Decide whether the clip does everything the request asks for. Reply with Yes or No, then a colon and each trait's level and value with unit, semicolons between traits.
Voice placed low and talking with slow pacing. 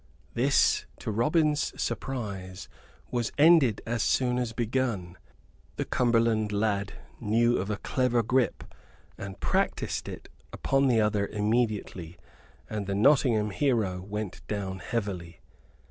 Yes: low, 110 Hz; slow, 120 wpm